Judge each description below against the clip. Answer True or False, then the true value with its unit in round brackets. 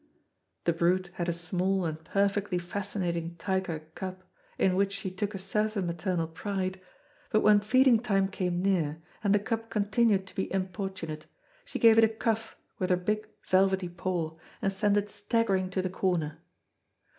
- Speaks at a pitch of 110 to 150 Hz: False (190 Hz)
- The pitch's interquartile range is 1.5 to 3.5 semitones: True (2.5 semitones)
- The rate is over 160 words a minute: True (170 wpm)